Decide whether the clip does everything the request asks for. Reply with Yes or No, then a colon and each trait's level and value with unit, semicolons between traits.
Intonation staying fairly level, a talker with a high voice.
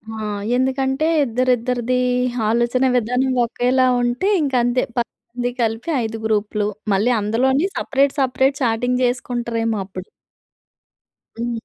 Yes: narrow, 2.3 semitones; high, 245 Hz